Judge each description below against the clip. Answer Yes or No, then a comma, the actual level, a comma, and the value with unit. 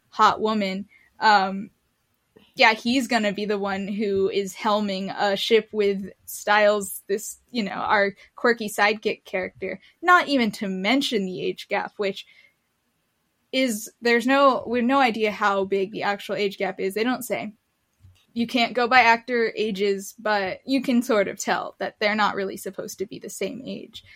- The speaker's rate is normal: Yes, average, 175 wpm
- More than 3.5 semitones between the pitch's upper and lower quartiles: No, average, 2.9 semitones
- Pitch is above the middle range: Yes, high, 210 Hz